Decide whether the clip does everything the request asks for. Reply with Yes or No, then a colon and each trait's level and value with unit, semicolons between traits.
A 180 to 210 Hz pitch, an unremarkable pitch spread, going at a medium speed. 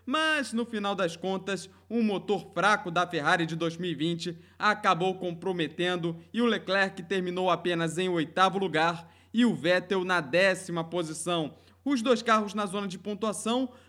Yes: medium, 185 Hz; average, 3.2 semitones; average, 150 wpm